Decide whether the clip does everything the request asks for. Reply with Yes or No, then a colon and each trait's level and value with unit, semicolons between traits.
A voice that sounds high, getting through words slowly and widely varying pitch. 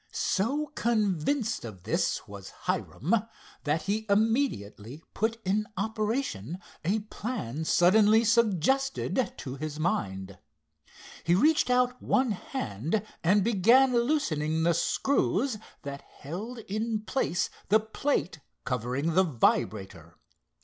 Yes: high, 200 Hz; slow, 110 wpm; wide, 7.2 semitones